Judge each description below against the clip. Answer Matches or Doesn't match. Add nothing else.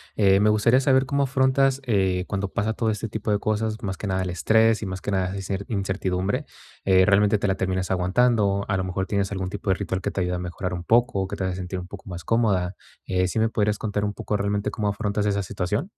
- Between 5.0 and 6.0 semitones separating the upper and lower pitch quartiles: Doesn't match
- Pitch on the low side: Matches